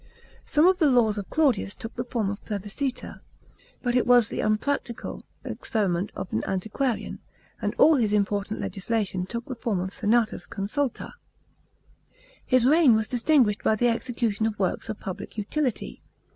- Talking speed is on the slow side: No, average, 160 wpm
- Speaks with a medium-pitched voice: No, high, 225 Hz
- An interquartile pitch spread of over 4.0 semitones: No, average, 3.6 semitones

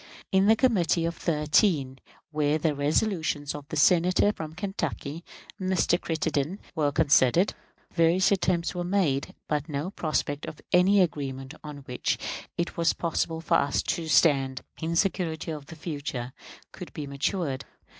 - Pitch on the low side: No, medium, 160 Hz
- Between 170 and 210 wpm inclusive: No, average, 145 wpm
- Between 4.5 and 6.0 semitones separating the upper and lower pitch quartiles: No, average, 3.6 semitones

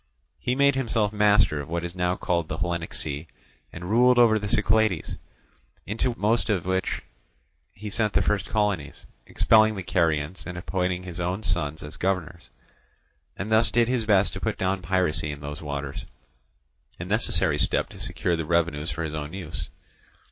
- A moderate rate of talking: Yes, average, 170 wpm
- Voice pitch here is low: Yes, very low, 90 Hz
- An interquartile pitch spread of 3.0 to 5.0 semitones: Yes, average, 4.4 semitones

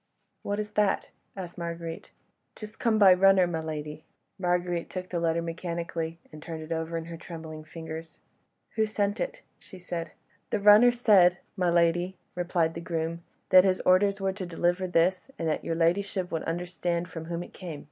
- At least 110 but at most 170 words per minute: No, average, 180 wpm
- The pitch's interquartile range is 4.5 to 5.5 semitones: No, narrow, 2.4 semitones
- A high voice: No, medium, 175 Hz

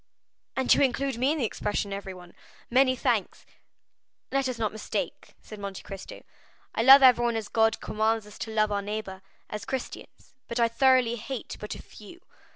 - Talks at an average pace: Yes, average, 170 wpm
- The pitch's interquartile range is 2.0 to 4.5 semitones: Yes, average, 3.6 semitones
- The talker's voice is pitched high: Yes, high, 225 Hz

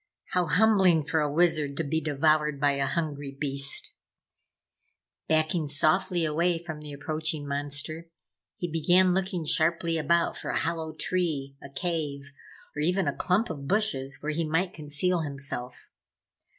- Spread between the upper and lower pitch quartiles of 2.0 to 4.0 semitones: Yes, average, 3.0 semitones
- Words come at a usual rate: Yes, average, 150 wpm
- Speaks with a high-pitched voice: No, medium, 155 Hz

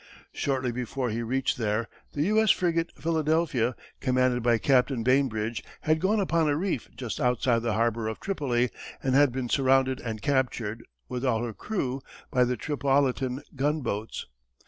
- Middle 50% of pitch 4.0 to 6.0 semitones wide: No, average, 3.4 semitones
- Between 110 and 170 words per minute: Yes, average, 155 wpm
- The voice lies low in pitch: Yes, low, 130 Hz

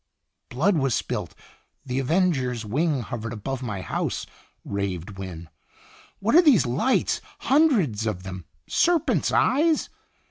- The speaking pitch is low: Yes, low, 125 Hz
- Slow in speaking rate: Yes, slow, 130 wpm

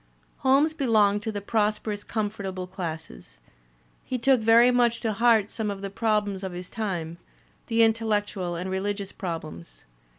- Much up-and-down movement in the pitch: No, average, 3.2 semitones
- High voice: Yes, high, 205 Hz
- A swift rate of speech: No, average, 145 wpm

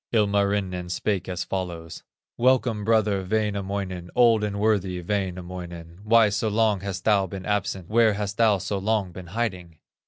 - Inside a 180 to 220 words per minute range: No, average, 150 wpm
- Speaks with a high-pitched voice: No, low, 100 Hz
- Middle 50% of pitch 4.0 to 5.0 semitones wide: No, average, 2.7 semitones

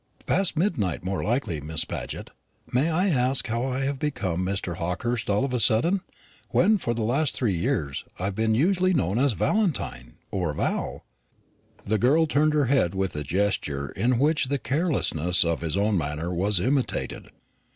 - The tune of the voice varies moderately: No, wide, 7.8 semitones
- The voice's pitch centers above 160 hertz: No, low, 115 Hz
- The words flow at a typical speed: Yes, average, 175 wpm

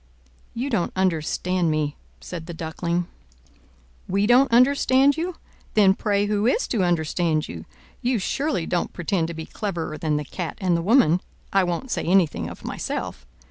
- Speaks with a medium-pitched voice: Yes, medium, 180 Hz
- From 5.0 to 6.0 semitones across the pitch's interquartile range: Yes, average, 5.3 semitones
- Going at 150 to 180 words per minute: Yes, average, 160 wpm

